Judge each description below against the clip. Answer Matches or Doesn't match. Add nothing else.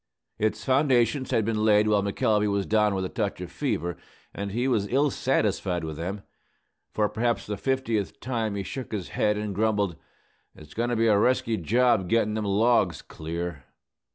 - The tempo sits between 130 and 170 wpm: Doesn't match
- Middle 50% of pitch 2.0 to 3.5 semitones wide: Matches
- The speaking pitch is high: Doesn't match